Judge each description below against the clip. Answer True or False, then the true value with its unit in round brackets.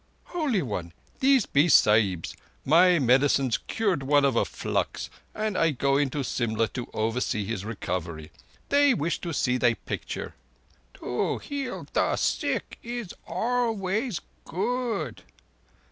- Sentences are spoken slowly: True (130 wpm)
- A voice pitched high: False (145 Hz)